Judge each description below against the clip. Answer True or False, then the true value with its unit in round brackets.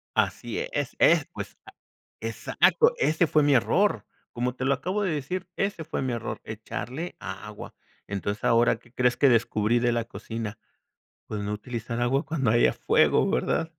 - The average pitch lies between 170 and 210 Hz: False (125 Hz)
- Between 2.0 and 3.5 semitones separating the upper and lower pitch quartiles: False (5.1 semitones)